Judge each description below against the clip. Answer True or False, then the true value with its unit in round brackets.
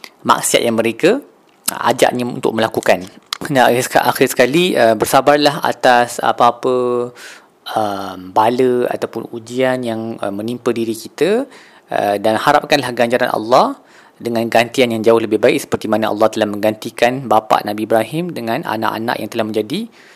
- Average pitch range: False (2.2 semitones)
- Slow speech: False (130 wpm)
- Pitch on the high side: False (115 Hz)